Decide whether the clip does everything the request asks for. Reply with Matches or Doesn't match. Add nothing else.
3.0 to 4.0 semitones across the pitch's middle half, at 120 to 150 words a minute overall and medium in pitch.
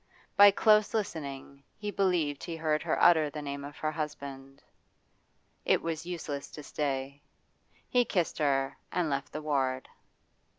Matches